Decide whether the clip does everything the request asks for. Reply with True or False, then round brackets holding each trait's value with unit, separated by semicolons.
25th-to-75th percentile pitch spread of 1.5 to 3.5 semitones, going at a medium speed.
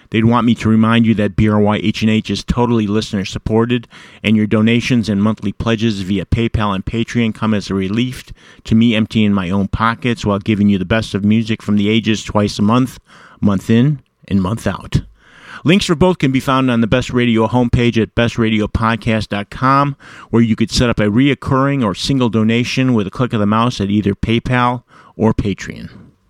True (2.5 semitones; 190 wpm)